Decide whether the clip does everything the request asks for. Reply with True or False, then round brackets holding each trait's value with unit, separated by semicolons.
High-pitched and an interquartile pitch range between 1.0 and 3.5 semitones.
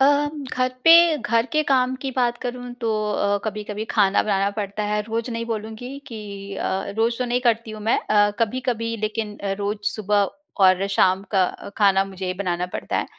True (220 Hz; 2.8 semitones)